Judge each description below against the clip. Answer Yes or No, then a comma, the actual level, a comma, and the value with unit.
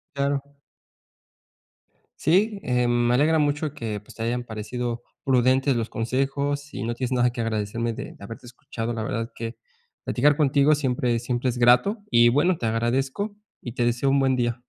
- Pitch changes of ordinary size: Yes, average, 3.0 semitones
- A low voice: Yes, low, 125 Hz